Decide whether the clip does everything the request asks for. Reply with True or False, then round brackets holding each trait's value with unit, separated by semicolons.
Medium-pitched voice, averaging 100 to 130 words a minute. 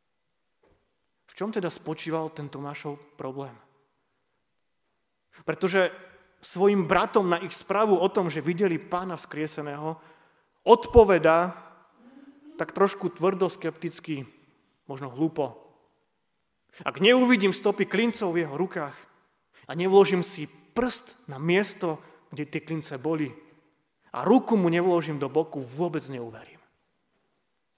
True (170 Hz; 110 wpm)